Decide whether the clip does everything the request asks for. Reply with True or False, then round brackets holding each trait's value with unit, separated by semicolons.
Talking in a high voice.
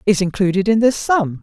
True (200 Hz)